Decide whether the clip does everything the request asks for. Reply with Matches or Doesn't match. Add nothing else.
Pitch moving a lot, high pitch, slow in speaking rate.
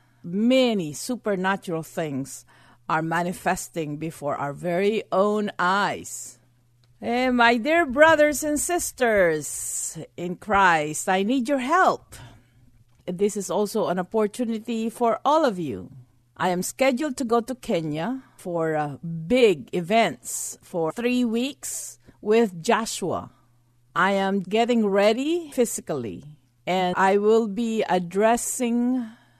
Matches